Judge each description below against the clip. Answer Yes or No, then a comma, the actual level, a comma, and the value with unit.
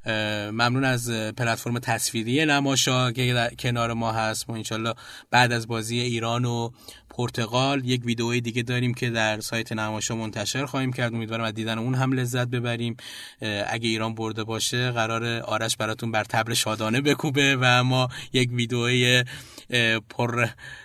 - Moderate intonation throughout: No, narrow, 1.7 semitones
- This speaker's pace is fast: No, average, 145 wpm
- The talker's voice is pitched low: Yes, low, 120 Hz